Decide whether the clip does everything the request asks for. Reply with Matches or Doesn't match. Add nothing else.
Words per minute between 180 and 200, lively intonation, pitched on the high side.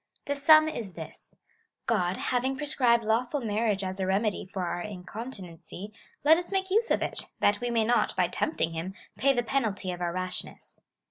Matches